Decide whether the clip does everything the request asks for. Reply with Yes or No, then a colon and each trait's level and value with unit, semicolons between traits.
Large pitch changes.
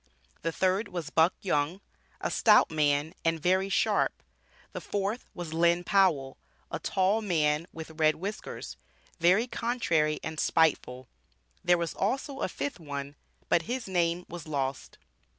No: average, 3.9 semitones